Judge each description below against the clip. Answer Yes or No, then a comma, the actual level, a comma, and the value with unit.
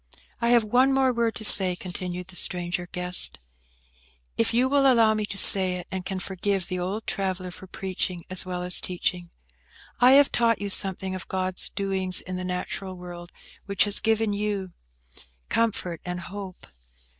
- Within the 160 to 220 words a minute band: Yes, average, 175 wpm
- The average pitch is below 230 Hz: Yes, high, 190 Hz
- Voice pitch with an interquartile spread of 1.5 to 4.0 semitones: Yes, average, 3.1 semitones